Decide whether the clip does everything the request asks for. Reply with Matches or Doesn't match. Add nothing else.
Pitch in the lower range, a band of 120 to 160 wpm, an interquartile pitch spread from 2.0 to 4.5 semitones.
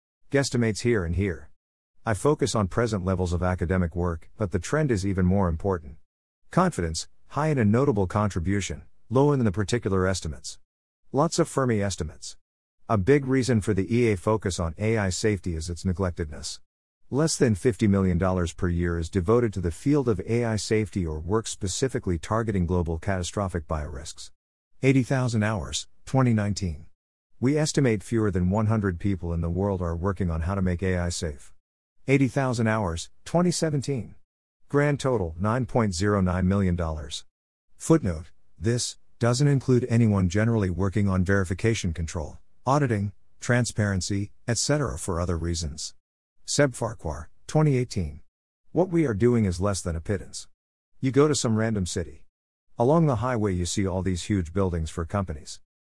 Doesn't match